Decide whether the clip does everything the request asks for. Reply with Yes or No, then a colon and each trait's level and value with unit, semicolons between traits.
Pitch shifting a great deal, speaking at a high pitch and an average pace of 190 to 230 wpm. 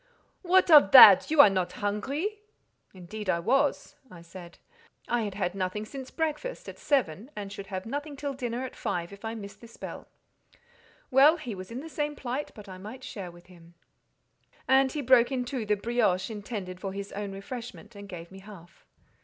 Yes: wide, 5.7 semitones; high, 215 Hz; average, 195 wpm